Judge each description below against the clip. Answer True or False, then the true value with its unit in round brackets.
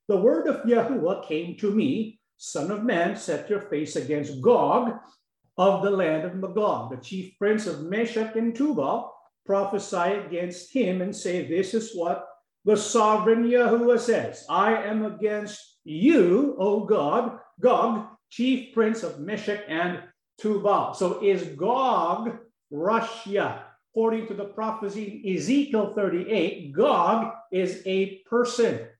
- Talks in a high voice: True (210 Hz)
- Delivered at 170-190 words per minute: False (140 wpm)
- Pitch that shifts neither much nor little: True (3.6 semitones)